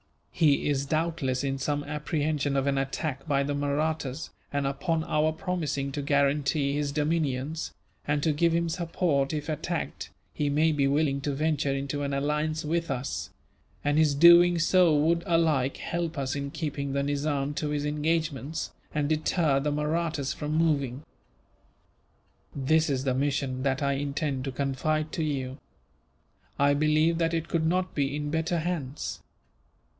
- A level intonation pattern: Yes, narrow, 2.3 semitones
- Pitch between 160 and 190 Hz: No, medium, 150 Hz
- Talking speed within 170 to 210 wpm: No, average, 160 wpm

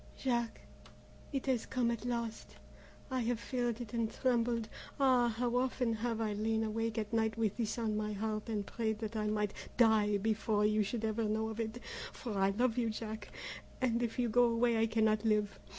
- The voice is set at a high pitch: Yes, high, 225 Hz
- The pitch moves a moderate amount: No, narrow, 1.7 semitones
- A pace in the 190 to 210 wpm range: Yes, average, 200 wpm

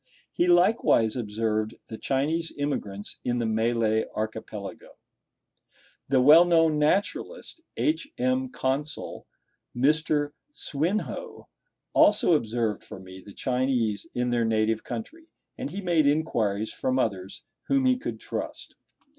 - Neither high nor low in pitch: No, low, 130 Hz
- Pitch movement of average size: No, wide, 7.4 semitones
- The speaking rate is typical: No, slow, 120 wpm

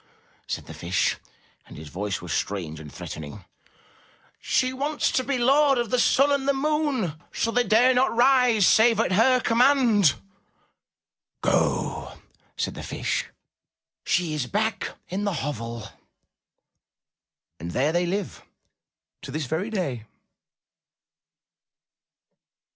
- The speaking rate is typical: No, slow, 125 wpm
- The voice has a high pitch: Yes, high, 215 Hz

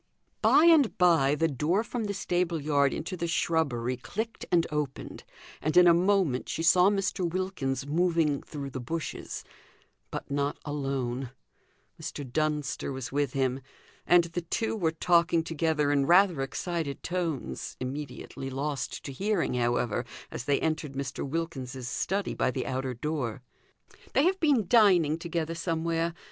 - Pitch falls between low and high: Yes, medium, 160 Hz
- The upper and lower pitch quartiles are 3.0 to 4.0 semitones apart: No, average, 4.5 semitones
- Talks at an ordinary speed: Yes, average, 150 wpm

